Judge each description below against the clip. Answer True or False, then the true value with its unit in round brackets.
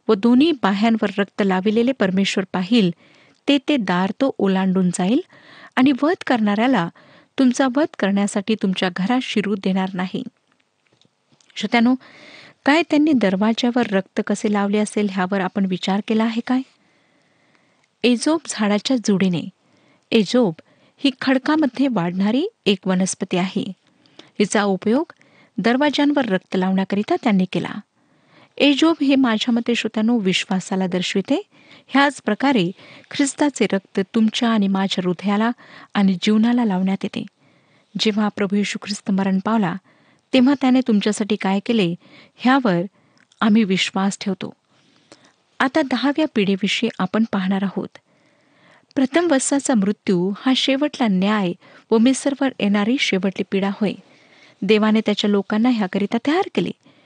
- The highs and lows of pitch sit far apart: False (4.9 semitones)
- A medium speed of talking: True (120 wpm)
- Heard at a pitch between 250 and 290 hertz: False (215 Hz)